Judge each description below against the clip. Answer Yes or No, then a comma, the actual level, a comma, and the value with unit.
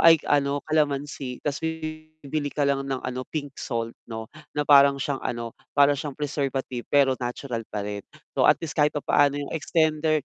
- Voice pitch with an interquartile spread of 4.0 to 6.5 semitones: No, narrow, 2.4 semitones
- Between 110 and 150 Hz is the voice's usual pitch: Yes, medium, 140 Hz